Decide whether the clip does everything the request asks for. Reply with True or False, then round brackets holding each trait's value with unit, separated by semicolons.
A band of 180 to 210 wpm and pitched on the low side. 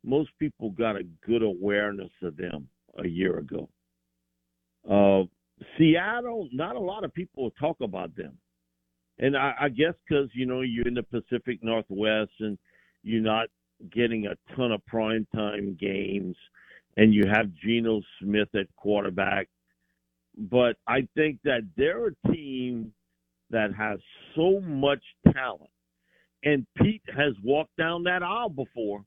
False (145 wpm; 110 Hz)